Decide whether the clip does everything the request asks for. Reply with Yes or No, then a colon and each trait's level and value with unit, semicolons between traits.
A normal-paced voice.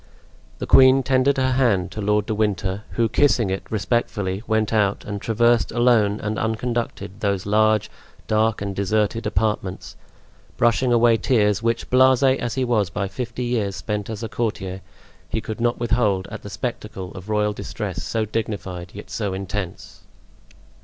Yes: average, 160 wpm